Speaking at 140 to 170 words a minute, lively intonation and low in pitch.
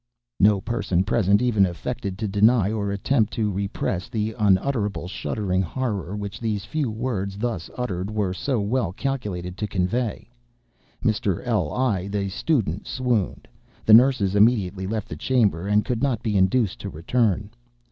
No: average, 150 wpm; average, 3.6 semitones; low, 105 Hz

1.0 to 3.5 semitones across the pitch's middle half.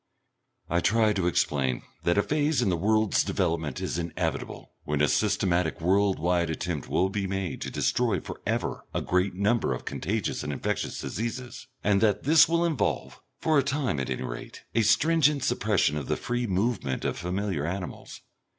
No: wide, 5.6 semitones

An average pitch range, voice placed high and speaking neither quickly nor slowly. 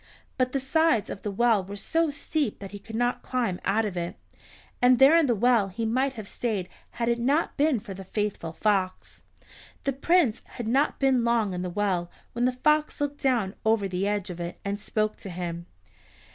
No: average, 4.7 semitones; high, 225 Hz; fast, 210 wpm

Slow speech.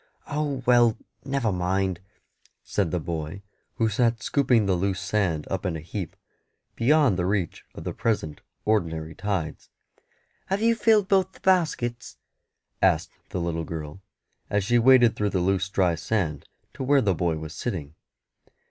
No: average, 155 wpm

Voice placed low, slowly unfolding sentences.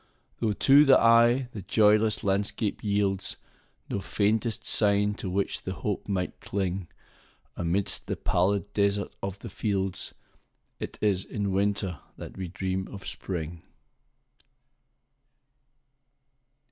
Yes: low, 100 Hz; slow, 110 wpm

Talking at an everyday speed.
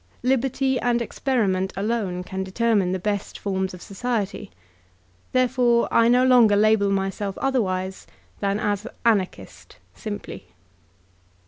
No: slow, 115 wpm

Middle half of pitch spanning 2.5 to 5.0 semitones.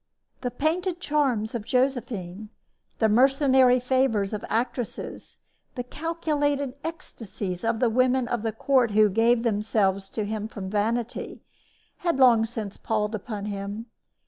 Yes: average, 3.7 semitones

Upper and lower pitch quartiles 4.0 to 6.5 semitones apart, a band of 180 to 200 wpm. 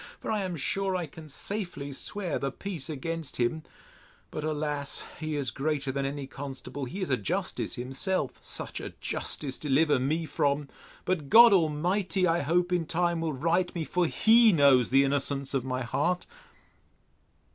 No: average, 4.4 semitones; average, 160 wpm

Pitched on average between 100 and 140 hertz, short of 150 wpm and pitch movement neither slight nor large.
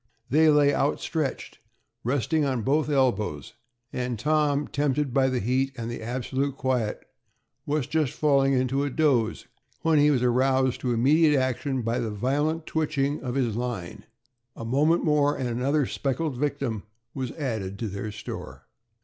No: low, 135 Hz; average, 155 wpm; average, 3.3 semitones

